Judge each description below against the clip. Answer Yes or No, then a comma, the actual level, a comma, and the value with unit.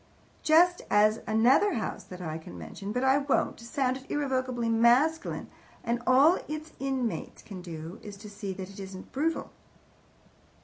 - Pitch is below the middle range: No, high, 235 Hz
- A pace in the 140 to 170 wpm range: Yes, average, 150 wpm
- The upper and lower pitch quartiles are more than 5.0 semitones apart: Yes, wide, 5.4 semitones